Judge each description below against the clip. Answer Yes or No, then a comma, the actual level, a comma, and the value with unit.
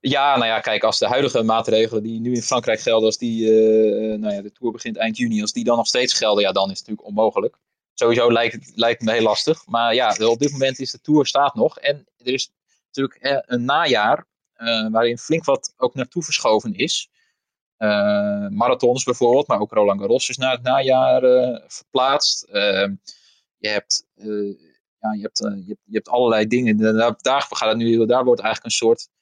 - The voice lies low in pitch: Yes, low, 120 Hz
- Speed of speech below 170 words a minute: No, average, 190 wpm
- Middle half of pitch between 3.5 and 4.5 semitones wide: Yes, average, 3.8 semitones